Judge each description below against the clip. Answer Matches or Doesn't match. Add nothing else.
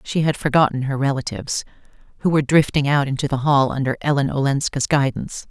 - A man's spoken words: Doesn't match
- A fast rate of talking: Doesn't match